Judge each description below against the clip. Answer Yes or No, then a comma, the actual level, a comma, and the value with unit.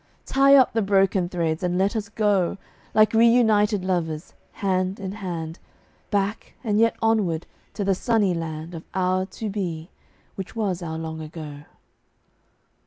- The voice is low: No, high, 190 Hz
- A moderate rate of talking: Yes, average, 150 wpm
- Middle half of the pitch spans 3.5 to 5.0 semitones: Yes, average, 3.9 semitones